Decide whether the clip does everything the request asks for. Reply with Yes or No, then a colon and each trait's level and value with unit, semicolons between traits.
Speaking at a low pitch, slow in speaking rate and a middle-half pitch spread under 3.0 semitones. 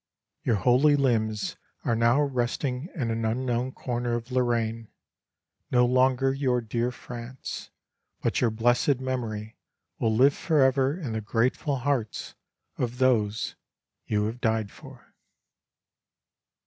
Yes: low, 120 Hz; slow, 120 wpm; narrow, 2.4 semitones